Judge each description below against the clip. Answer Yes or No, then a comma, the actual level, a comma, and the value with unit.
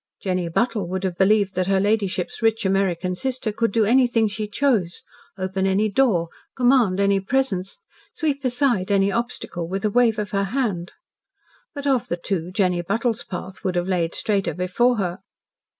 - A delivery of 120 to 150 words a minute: No, average, 170 wpm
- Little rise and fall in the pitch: No, average, 4.0 semitones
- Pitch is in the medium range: No, high, 200 Hz